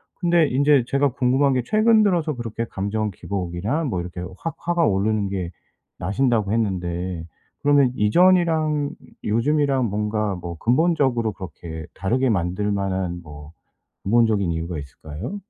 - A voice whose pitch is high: No, low, 110 Hz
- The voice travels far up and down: Yes, wide, 7.4 semitones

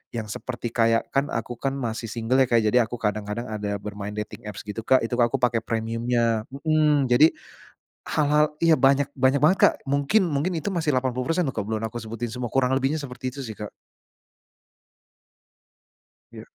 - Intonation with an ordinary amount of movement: Yes, average, 3.8 semitones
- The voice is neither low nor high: No, low, 125 Hz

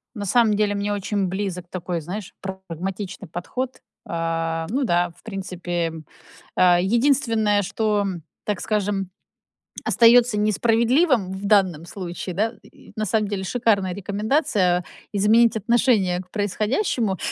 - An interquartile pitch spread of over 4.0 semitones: No, average, 3.4 semitones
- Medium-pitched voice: No, high, 200 Hz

